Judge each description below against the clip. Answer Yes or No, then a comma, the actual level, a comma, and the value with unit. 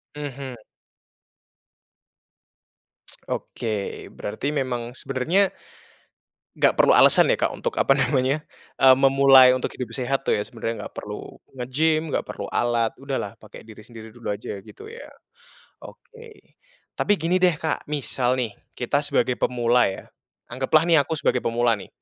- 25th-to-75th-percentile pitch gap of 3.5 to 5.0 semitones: Yes, average, 4.0 semitones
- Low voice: Yes, low, 130 Hz